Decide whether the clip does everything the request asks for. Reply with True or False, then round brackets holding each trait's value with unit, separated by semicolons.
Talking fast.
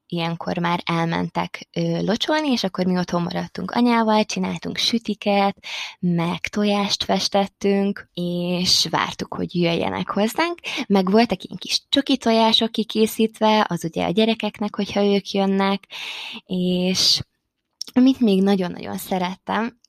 False (120 wpm)